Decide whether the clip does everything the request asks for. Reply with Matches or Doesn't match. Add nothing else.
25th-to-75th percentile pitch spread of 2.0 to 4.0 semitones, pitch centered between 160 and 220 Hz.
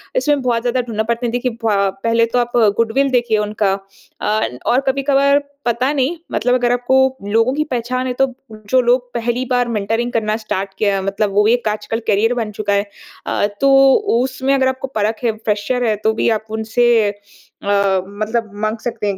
Doesn't match